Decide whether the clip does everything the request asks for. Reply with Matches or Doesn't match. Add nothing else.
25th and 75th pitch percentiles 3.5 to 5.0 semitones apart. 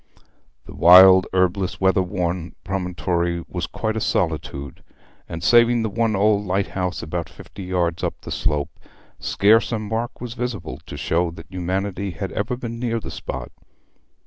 Matches